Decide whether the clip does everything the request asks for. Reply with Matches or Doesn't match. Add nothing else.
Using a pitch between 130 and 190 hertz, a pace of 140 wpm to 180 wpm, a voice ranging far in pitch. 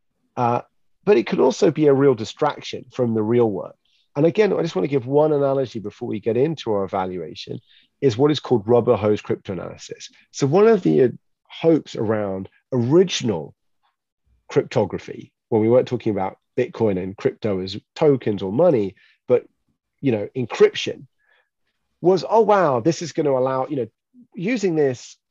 Matches